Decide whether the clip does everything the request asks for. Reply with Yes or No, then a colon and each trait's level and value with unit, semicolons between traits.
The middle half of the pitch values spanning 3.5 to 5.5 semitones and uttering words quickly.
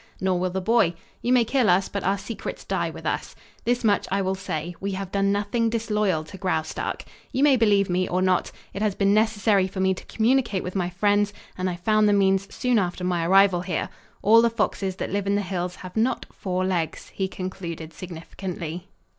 No: narrow, 2.5 semitones; fast, 215 wpm